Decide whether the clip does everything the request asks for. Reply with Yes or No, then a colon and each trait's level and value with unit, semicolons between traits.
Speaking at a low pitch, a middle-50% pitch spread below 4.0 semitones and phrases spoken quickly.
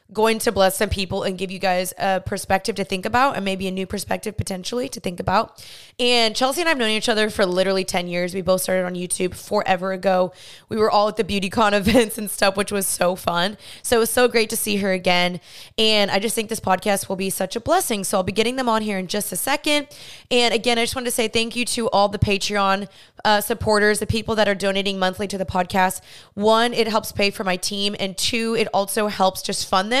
No: high, 205 Hz; average, 3.0 semitones; fast, 250 wpm